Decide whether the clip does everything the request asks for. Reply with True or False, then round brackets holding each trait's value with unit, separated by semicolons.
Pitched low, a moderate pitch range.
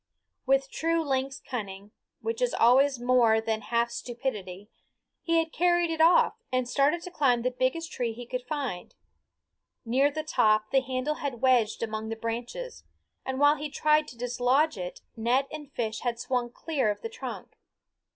False (255 Hz; 4.4 semitones)